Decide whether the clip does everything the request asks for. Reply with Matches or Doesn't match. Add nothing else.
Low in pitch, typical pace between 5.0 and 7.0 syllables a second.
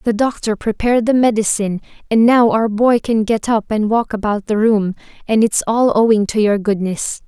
Doesn't match